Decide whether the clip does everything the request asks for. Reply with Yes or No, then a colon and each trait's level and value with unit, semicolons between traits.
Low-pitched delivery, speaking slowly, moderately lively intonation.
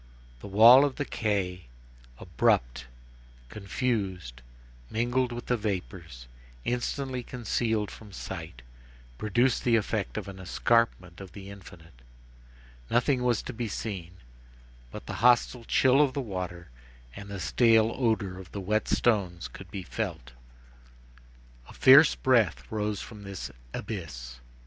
Yes: low, 105 Hz; slow, 130 wpm; average, 4.9 semitones